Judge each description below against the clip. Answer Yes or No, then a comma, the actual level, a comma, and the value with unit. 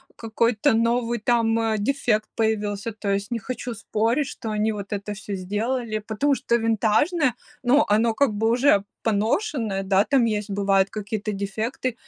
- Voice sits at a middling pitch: No, high, 220 Hz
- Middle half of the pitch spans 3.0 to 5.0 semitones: No, narrow, 2.5 semitones